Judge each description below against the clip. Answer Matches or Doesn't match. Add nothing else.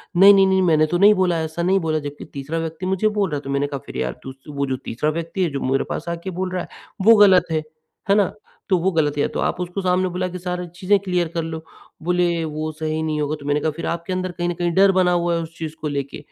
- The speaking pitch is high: Doesn't match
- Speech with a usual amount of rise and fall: Matches